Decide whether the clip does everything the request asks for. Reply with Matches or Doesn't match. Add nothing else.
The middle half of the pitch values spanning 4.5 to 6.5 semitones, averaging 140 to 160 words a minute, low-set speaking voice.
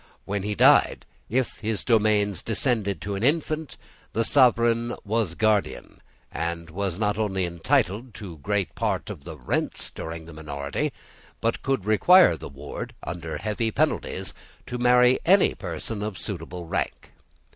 Matches